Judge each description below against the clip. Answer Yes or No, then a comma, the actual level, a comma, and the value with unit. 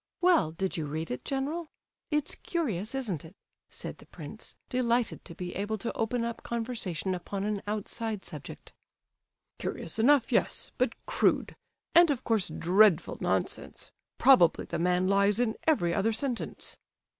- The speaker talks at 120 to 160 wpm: Yes, average, 150 wpm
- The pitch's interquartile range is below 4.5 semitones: No, wide, 5.5 semitones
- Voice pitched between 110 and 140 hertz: No, high, 215 Hz